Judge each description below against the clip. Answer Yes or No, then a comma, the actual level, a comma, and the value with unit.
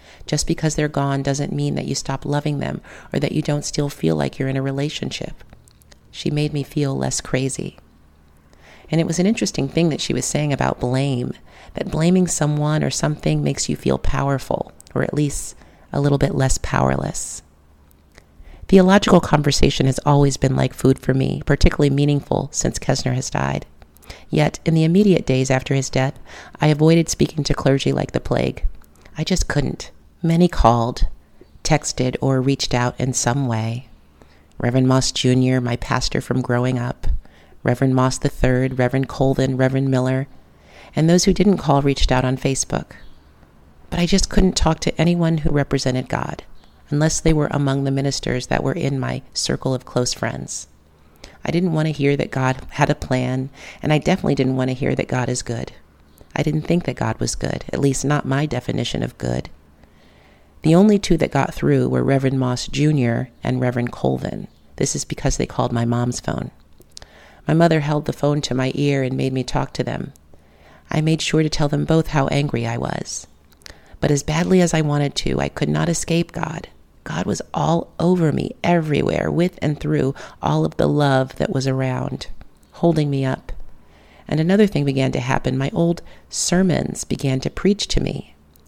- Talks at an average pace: Yes, average, 185 wpm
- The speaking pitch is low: Yes, low, 130 Hz